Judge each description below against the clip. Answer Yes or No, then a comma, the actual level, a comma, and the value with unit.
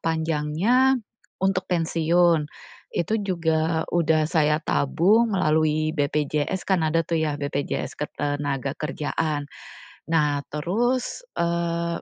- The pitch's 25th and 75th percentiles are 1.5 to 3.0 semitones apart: Yes, narrow, 2.5 semitones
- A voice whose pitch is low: No, medium, 160 Hz